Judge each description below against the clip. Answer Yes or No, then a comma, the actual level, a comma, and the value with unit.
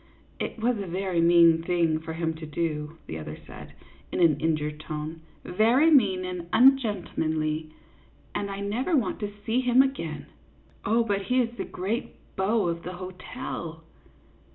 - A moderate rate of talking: Yes, average, 170 wpm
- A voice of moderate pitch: Yes, medium, 180 Hz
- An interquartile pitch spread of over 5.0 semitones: Yes, wide, 5.6 semitones